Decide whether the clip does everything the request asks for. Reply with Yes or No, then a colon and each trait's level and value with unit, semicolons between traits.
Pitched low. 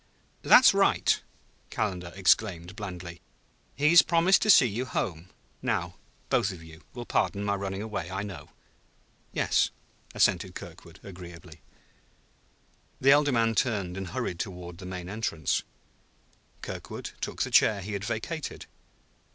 Yes: low, 100 Hz